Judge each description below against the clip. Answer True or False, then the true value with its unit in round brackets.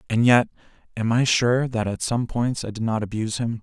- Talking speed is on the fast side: True (230 wpm)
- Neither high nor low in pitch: False (115 Hz)